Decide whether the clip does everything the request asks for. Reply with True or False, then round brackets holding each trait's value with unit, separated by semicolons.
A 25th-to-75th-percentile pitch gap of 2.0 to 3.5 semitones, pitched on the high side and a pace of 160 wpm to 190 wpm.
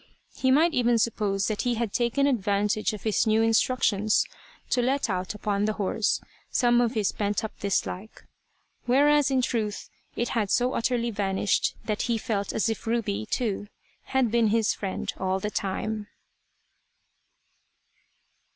False (2.8 semitones; 220 Hz; 150 wpm)